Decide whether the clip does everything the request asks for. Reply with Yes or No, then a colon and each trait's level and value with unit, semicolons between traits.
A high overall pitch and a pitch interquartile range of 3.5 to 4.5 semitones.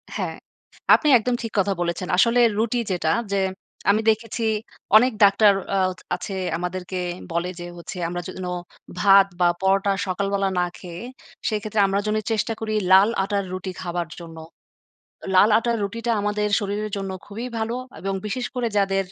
No: high, 200 Hz; average, 2.8 semitones